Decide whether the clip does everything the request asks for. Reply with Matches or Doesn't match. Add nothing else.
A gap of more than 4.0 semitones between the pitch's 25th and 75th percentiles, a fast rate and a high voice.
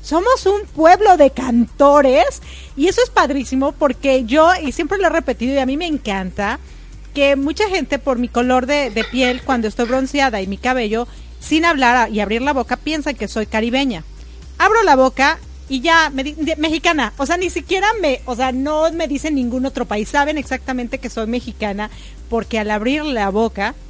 Matches